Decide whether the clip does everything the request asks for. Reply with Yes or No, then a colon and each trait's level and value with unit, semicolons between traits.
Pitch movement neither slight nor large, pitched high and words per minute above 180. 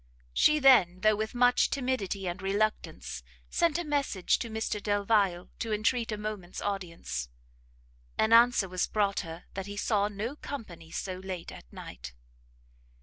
No: average, 3.8 semitones; high, 205 Hz; average, 150 wpm